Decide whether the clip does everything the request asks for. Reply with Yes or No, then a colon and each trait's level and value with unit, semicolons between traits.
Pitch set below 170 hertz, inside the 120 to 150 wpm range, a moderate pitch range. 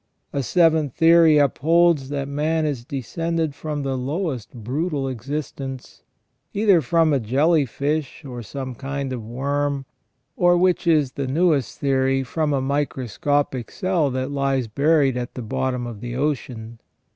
Yes: medium, 140 Hz; average, 145 wpm; average, 3.2 semitones